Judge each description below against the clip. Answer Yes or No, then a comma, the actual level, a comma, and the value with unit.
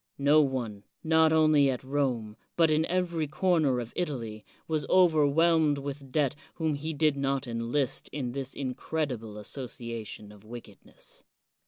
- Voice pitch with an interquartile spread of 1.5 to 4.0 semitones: No, average, 4.4 semitones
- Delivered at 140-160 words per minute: Yes, average, 145 wpm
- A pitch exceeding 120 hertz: Yes, medium, 140 Hz